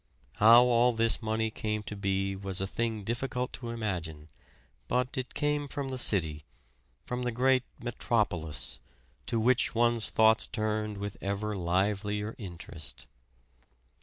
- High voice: No, low, 110 Hz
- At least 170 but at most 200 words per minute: No, slow, 135 wpm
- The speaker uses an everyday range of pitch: Yes, average, 3.6 semitones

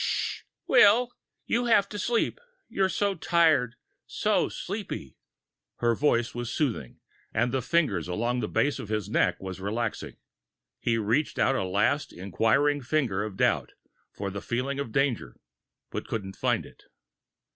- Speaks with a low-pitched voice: Yes, low, 120 Hz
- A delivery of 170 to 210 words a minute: No, average, 150 wpm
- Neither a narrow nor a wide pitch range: No, wide, 6.1 semitones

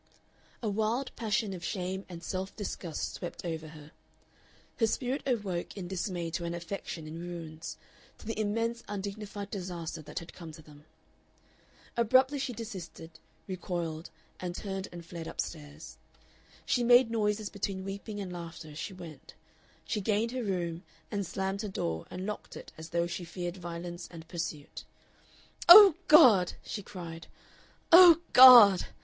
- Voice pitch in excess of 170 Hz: Yes, medium, 185 Hz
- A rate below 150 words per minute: No, average, 155 wpm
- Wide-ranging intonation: No, average, 4.1 semitones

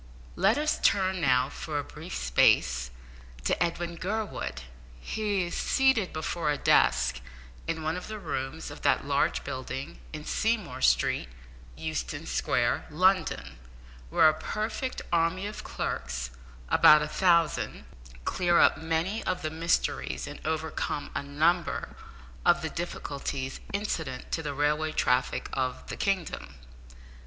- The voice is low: No, medium, 160 Hz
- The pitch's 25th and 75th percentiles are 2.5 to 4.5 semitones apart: No, wide, 5.4 semitones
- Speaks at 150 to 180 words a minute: No, slow, 135 wpm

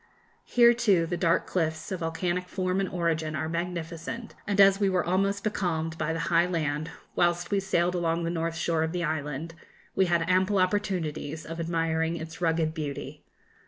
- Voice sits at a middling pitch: Yes, medium, 170 Hz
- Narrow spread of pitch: Yes, narrow, 2.2 semitones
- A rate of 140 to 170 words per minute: No, average, 180 wpm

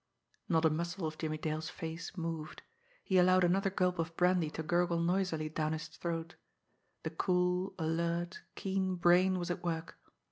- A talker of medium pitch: Yes, medium, 170 Hz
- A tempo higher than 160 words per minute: Yes, average, 170 wpm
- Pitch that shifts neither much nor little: No, narrow, 2.1 semitones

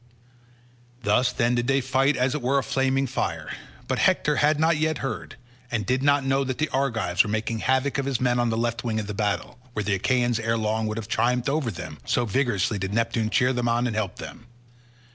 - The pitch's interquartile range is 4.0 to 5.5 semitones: No, average, 3.3 semitones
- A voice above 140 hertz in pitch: No, low, 120 Hz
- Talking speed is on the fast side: Yes, fast, 225 wpm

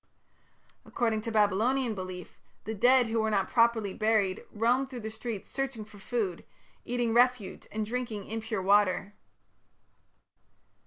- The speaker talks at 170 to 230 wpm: No, slow, 135 wpm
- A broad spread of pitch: No, average, 2.9 semitones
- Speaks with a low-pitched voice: No, high, 220 Hz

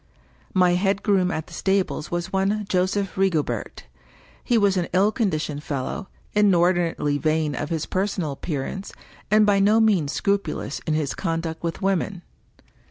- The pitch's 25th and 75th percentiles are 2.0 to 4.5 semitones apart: Yes, average, 3.8 semitones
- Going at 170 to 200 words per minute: No, average, 150 wpm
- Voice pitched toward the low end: No, medium, 185 Hz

